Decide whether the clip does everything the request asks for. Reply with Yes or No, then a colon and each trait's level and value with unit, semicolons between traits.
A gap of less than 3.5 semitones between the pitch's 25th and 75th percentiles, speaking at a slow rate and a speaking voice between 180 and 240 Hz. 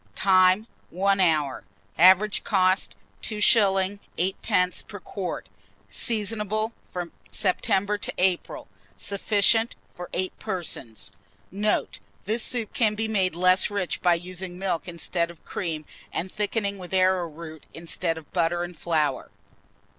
Yes: average, 2.8 semitones; slow, 125 wpm; medium, 185 Hz